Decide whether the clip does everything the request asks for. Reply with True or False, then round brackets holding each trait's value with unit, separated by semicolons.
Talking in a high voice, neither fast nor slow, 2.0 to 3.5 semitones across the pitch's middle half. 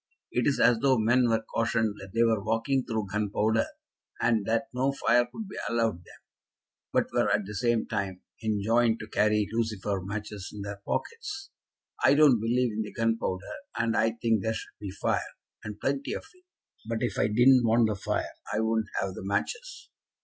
False (115 Hz; 190 wpm; 2.4 semitones)